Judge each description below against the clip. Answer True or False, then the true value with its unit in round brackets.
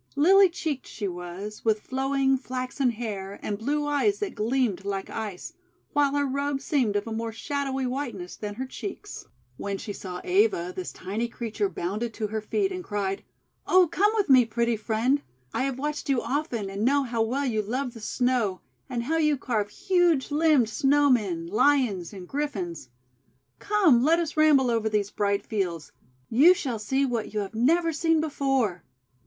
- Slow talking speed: False (180 wpm)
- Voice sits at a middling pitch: False (245 Hz)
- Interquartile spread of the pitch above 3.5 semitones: True (5.5 semitones)